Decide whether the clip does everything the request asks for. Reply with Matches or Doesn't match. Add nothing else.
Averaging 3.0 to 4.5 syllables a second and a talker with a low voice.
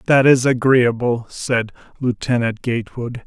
Matches